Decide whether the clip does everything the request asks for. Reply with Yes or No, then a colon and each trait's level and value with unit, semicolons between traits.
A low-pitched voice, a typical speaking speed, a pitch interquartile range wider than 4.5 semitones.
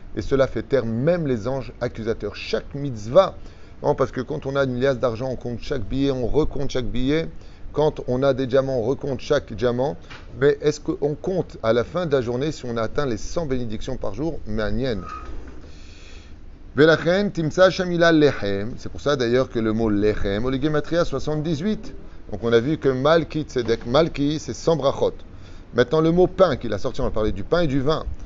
Yes: low, 130 Hz; average, 200 wpm; average, 5.1 semitones